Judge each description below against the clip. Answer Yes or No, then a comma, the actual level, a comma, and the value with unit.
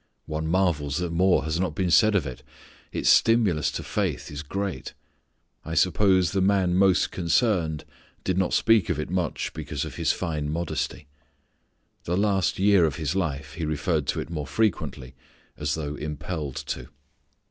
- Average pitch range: Yes, average, 3.8 semitones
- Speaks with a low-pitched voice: Yes, very low, 85 Hz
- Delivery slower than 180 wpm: Yes, average, 170 wpm